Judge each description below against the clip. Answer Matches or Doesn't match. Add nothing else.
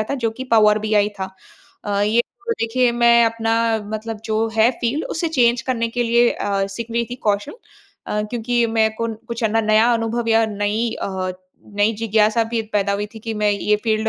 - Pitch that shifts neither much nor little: Doesn't match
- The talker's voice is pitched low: Doesn't match